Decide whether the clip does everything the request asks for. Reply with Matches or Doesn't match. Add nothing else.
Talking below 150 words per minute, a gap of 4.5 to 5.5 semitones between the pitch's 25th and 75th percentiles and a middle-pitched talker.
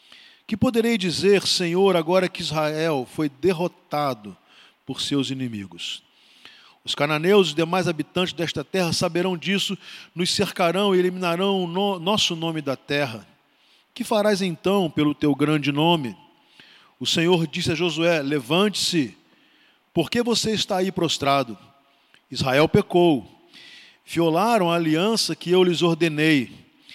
Doesn't match